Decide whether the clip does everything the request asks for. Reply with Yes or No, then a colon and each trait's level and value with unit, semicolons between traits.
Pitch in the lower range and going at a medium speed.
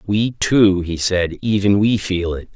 Yes: low, 100 Hz; average, 190 wpm